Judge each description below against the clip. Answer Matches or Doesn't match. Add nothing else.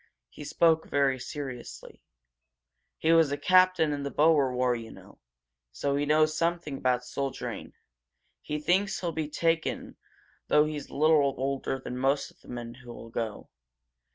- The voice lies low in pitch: Doesn't match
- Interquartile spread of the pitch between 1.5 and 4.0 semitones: Matches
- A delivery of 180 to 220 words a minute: Doesn't match